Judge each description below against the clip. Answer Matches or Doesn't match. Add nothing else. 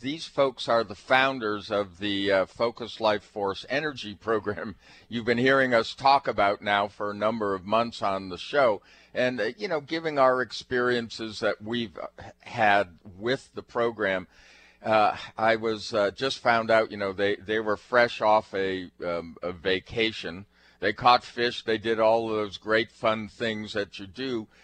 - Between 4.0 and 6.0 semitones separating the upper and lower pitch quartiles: Doesn't match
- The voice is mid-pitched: Doesn't match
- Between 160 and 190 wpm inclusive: Matches